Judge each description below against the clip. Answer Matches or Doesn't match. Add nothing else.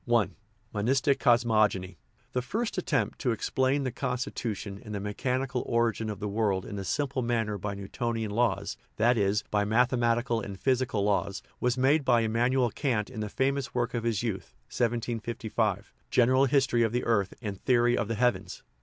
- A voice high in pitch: Doesn't match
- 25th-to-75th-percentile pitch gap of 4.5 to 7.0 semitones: Doesn't match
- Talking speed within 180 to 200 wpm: Doesn't match